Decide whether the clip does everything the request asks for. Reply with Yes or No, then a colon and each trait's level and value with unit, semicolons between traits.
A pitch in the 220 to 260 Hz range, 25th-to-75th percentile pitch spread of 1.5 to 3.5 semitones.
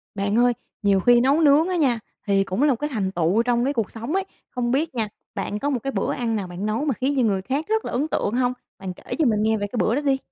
No: high, 240 Hz; average, 5.2 semitones